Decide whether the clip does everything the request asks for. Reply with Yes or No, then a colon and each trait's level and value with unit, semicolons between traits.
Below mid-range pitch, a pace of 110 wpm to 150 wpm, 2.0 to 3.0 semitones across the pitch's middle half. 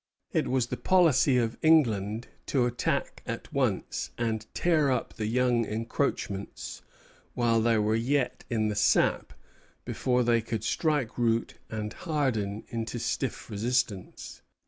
Yes: low, 115 Hz; slow, 135 wpm; average, 2.7 semitones